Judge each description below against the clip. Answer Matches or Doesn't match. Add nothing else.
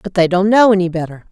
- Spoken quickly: Matches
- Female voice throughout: Matches